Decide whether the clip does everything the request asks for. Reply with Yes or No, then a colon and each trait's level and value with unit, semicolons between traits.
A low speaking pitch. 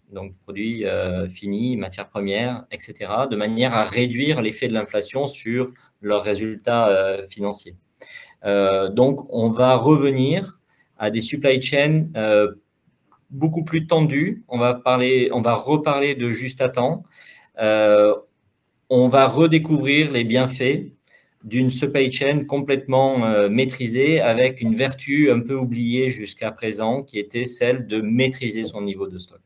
Yes: low, 125 Hz